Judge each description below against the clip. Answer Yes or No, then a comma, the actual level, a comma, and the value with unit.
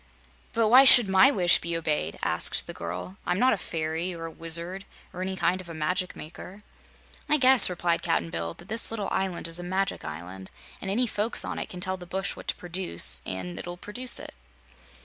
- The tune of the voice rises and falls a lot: No, average, 3.5 semitones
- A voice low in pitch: No, medium, 180 Hz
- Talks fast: Yes, fast, 210 wpm